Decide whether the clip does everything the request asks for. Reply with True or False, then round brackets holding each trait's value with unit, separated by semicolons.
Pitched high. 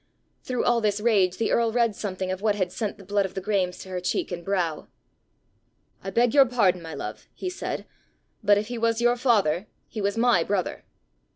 True (205 Hz)